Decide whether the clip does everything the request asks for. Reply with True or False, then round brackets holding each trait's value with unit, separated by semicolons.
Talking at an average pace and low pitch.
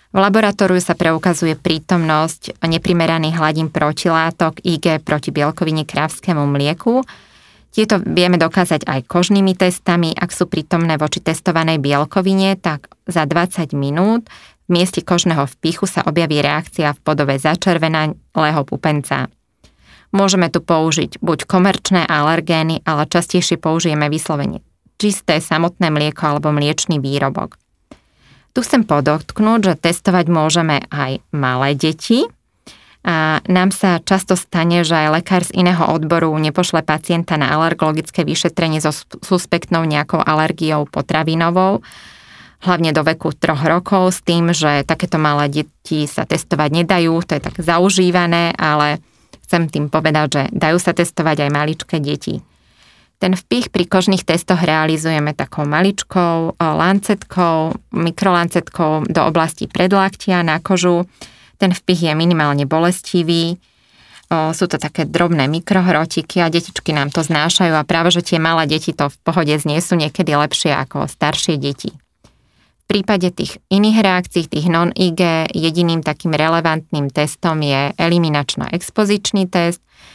False (135 wpm; 165 Hz)